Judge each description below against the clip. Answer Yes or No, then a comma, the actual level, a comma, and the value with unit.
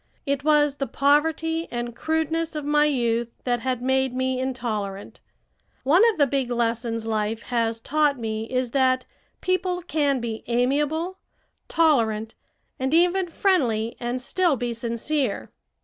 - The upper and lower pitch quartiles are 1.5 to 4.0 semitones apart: No, average, 4.5 semitones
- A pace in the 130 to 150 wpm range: Yes, average, 140 wpm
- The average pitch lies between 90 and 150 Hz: No, very high, 260 Hz